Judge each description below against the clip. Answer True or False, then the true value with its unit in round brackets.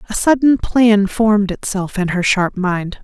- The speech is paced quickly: False (180 wpm)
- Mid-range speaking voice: False (205 Hz)